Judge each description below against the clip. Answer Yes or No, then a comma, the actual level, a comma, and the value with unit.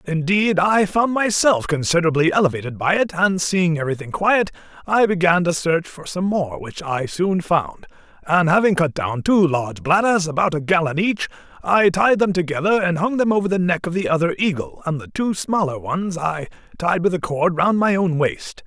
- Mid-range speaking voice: Yes, medium, 175 Hz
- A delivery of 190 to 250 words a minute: Yes, average, 200 wpm